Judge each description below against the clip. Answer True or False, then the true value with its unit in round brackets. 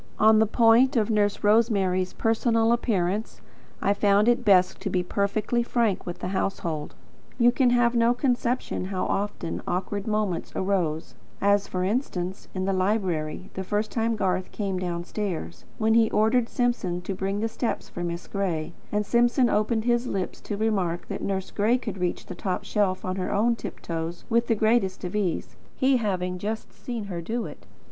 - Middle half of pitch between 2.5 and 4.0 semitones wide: True (3.7 semitones)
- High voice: True (205 Hz)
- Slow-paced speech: False (180 wpm)